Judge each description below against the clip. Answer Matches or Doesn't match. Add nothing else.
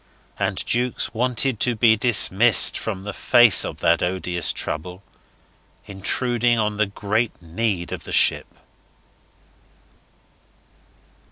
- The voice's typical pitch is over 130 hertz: Doesn't match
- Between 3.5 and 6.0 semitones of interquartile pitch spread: Matches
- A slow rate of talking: Matches